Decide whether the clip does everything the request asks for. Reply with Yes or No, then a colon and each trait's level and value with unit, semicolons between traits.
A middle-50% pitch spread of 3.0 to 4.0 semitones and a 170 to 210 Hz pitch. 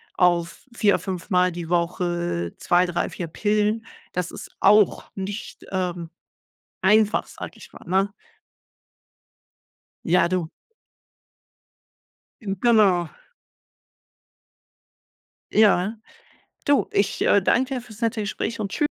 Yes: average, 3.3 semitones; high, 190 Hz